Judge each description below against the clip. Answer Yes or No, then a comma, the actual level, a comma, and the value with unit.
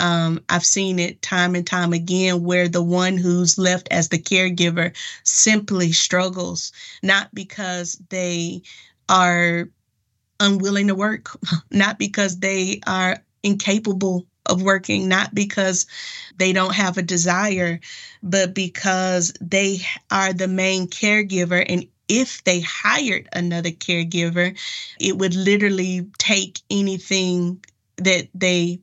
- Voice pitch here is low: No, medium, 185 Hz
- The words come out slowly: Yes, slow, 125 wpm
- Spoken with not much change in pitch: Yes, narrow, 1.7 semitones